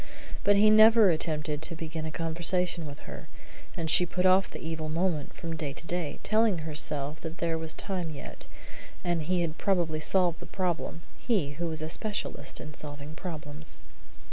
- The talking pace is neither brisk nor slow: Yes, average, 180 wpm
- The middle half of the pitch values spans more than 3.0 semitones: No, average, 2.7 semitones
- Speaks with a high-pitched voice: No, medium, 165 Hz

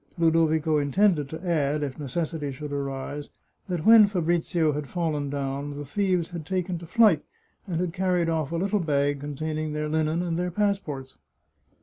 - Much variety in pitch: No, average, 3.3 semitones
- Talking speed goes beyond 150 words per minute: Yes, average, 165 wpm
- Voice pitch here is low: No, medium, 160 Hz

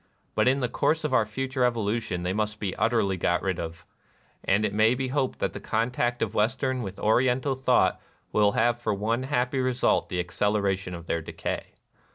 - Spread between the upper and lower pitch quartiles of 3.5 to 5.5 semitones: Yes, average, 4.2 semitones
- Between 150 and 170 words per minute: No, average, 195 wpm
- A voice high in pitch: No, low, 110 Hz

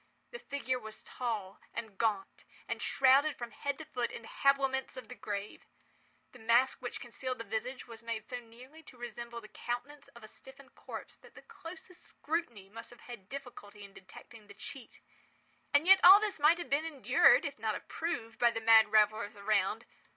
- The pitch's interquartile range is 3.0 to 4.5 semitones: Yes, average, 4.1 semitones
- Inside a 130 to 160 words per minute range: No, average, 190 wpm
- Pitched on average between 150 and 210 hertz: No, high, 240 Hz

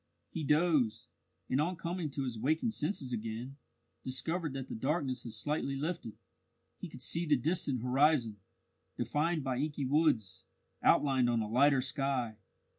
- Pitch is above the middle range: No, low, 135 Hz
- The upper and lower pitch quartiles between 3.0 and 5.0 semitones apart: Yes, average, 3.8 semitones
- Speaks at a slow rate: No, average, 150 wpm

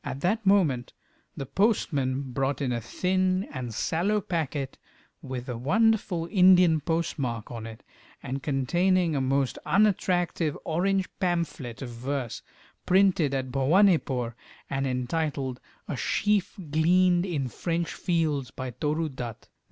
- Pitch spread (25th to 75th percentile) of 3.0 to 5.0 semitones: No, wide, 5.6 semitones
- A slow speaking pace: Yes, slow, 130 wpm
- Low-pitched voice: No, medium, 150 Hz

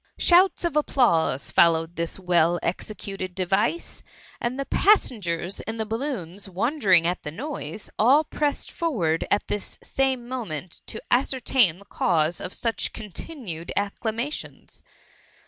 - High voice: Yes, high, 205 Hz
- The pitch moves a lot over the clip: Yes, wide, 7.1 semitones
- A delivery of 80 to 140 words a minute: Yes, slow, 135 wpm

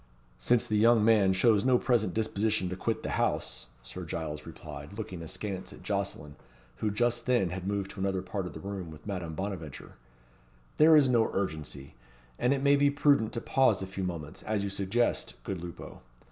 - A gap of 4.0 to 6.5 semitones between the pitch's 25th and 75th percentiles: Yes, average, 4.4 semitones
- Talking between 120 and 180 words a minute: No, average, 190 wpm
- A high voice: No, low, 100 Hz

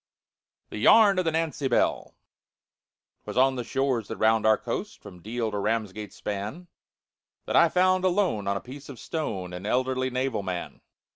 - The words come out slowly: No, average, 175 wpm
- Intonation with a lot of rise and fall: Yes, wide, 5.7 semitones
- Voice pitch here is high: No, low, 125 Hz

